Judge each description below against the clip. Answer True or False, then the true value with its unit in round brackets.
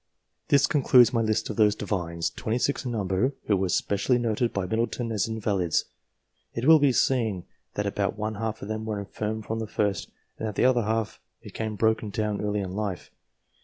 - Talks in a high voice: False (110 Hz)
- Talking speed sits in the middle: True (195 wpm)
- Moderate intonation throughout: False (2.2 semitones)